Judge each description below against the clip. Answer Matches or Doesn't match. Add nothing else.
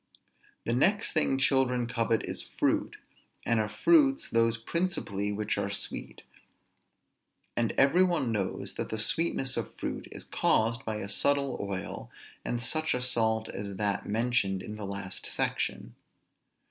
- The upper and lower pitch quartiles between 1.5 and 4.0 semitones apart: Doesn't match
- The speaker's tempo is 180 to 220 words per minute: Doesn't match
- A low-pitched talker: Matches